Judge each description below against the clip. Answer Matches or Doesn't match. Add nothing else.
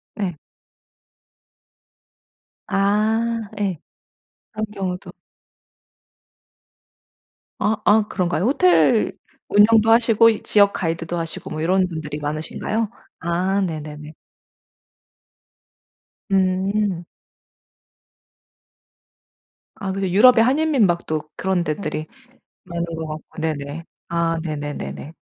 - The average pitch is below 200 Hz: Matches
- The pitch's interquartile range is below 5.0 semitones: Matches